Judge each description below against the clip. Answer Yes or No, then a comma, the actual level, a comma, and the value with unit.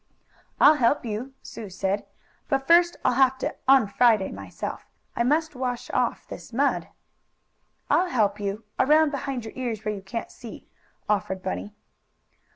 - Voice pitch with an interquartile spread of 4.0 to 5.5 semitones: Yes, average, 4.7 semitones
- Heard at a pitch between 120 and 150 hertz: No, high, 240 Hz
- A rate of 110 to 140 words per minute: No, average, 155 wpm